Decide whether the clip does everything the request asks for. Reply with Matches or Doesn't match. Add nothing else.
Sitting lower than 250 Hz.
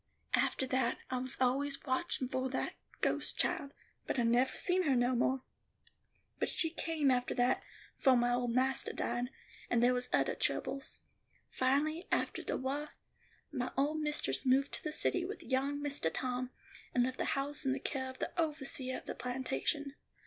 Doesn't match